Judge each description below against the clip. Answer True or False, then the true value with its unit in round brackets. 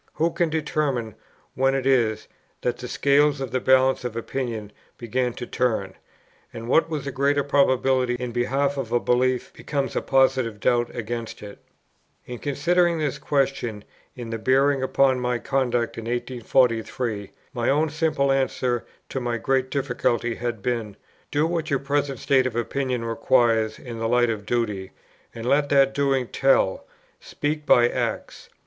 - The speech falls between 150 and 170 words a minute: True (160 wpm)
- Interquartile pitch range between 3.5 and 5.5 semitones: False (2.8 semitones)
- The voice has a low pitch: True (130 Hz)